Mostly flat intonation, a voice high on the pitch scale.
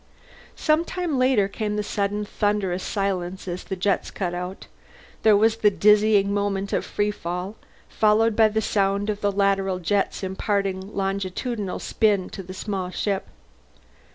Yes: narrow, 1.7 semitones; high, 200 Hz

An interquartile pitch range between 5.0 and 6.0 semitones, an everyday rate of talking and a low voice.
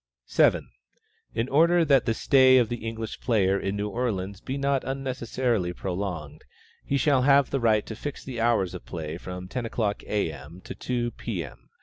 Yes: average, 5.3 semitones; average, 195 wpm; low, 115 Hz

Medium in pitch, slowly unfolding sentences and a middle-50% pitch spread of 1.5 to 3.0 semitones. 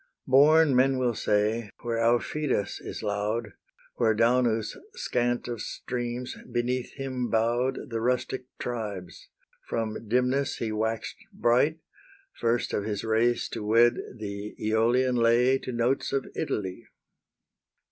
No: low, 120 Hz; slow, 125 wpm; narrow, 2.4 semitones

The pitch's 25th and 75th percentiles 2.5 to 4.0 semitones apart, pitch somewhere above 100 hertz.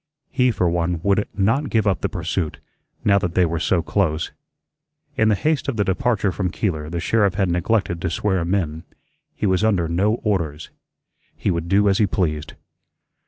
No: average, 3.6 semitones; very low, 95 Hz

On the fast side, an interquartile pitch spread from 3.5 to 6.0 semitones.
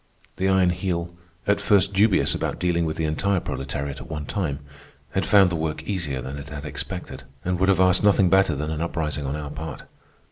Yes: fast, 210 wpm; average, 4.1 semitones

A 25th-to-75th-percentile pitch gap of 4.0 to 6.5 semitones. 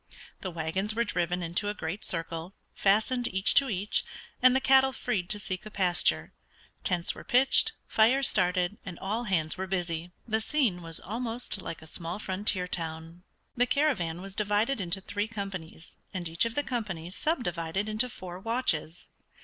Yes: average, 4.5 semitones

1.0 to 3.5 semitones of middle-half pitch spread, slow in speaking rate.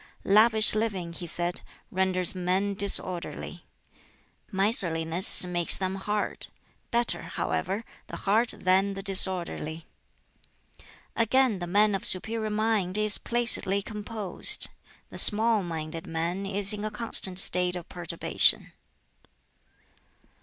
Yes: average, 3.0 semitones; slow, 110 wpm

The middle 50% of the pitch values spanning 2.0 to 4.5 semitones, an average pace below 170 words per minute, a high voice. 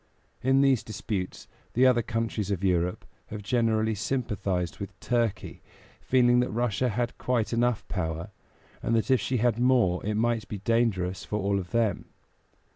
No: average, 3.7 semitones; average, 160 wpm; low, 110 Hz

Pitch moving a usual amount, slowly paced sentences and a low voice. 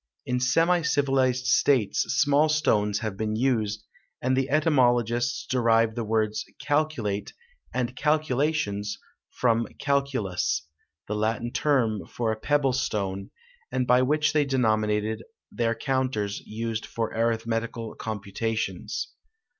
Yes: average, 3.8 semitones; slow, 115 wpm; low, 120 Hz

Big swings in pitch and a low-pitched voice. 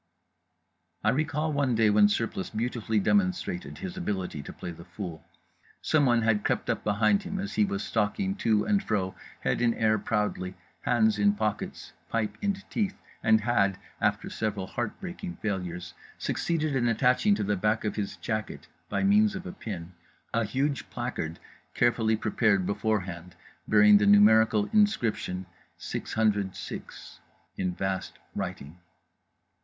Yes: wide, 6.1 semitones; low, 110 Hz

